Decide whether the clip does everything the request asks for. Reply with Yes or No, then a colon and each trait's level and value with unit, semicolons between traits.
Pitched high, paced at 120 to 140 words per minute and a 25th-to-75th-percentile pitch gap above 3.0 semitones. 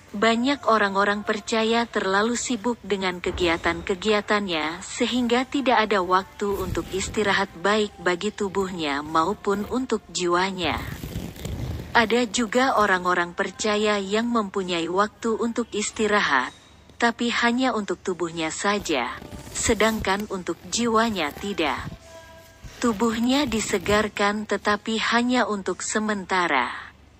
No: high, 205 Hz; average, 95 wpm; average, 3.5 semitones